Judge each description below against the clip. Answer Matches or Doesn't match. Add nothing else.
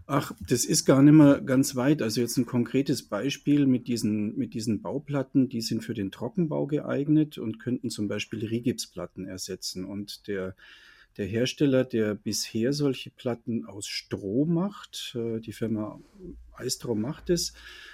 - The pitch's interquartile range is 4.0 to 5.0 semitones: Matches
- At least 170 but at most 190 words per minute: Doesn't match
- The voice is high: Doesn't match